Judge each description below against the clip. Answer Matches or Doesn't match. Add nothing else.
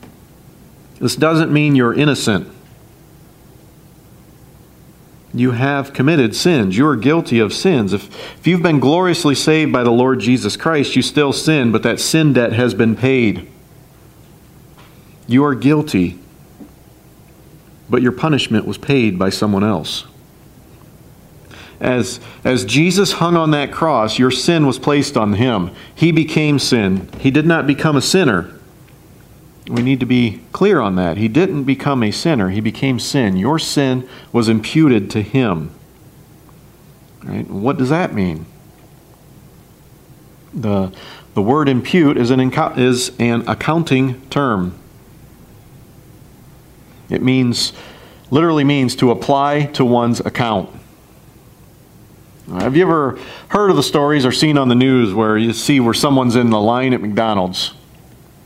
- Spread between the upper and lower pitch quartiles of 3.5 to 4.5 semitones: Matches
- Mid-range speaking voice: Doesn't match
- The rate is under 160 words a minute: Matches